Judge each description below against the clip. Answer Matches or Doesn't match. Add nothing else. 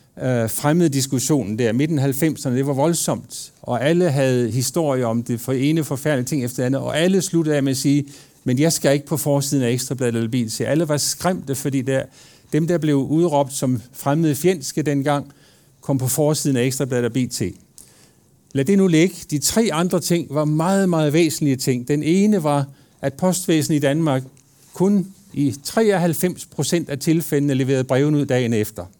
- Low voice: Doesn't match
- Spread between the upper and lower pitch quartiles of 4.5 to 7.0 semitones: Doesn't match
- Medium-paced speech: Matches